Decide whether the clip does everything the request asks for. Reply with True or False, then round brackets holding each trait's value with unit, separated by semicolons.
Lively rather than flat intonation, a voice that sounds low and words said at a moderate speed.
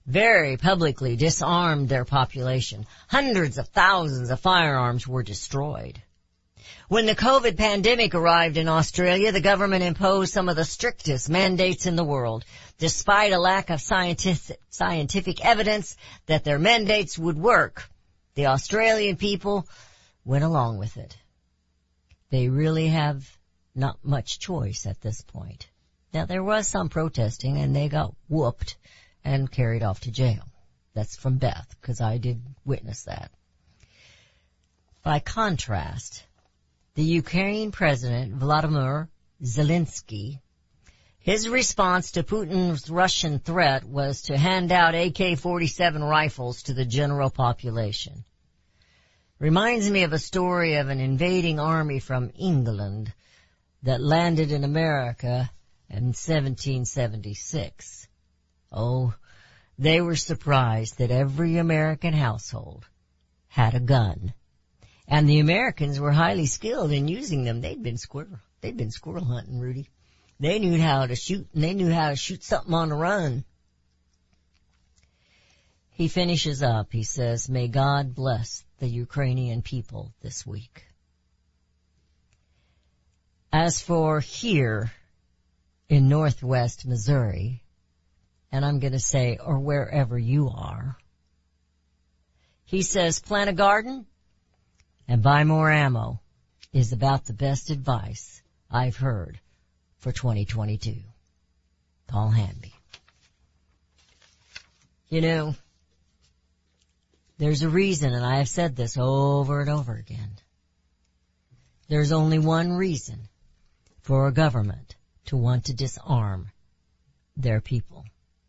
False (8.1 semitones; 130 Hz; 120 wpm)